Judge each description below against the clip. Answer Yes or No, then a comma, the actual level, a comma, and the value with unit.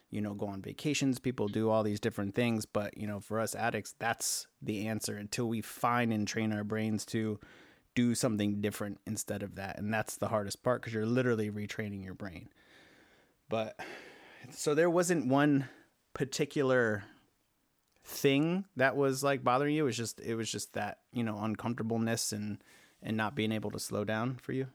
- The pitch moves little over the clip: No, average, 3.5 semitones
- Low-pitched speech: Yes, low, 110 Hz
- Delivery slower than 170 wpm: No, average, 185 wpm